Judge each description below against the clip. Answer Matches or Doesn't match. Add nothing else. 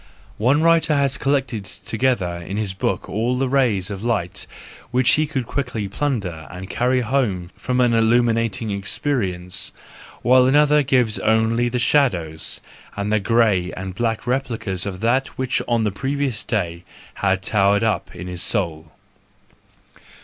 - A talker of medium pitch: Doesn't match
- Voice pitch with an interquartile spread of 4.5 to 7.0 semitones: Matches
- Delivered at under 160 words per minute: Matches